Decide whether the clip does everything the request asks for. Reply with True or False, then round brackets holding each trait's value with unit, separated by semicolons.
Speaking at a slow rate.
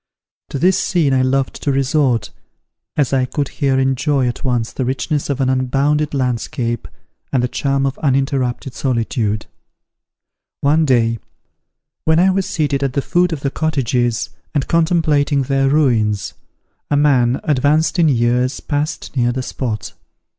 False (150 wpm)